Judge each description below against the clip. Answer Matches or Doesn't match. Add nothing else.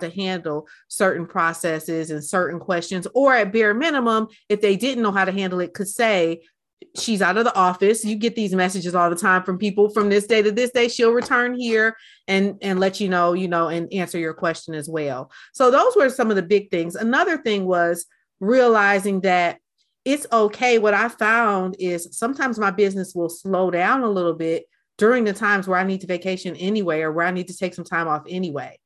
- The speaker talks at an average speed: Doesn't match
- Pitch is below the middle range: Doesn't match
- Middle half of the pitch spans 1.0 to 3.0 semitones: Doesn't match